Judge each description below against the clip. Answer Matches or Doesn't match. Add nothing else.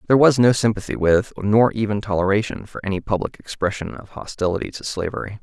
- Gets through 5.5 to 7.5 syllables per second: Matches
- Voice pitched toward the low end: Matches